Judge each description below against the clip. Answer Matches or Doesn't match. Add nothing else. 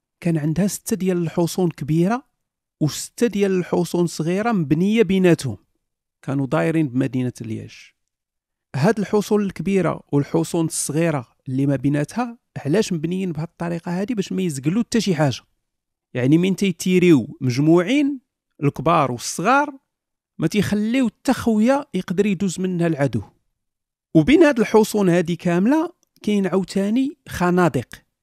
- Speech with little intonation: Doesn't match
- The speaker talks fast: Doesn't match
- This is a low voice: Doesn't match